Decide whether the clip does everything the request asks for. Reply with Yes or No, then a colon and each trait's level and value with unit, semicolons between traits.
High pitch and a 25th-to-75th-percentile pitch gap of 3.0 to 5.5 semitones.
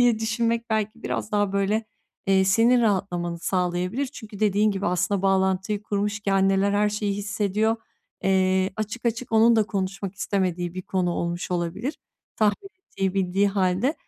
No: high, 200 Hz; narrow, 2.4 semitones